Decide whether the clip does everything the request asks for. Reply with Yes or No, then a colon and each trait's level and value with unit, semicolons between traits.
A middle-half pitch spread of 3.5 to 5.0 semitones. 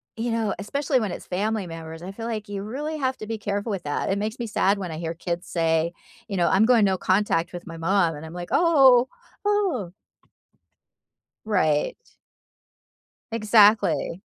Yes: average, 4.7 semitones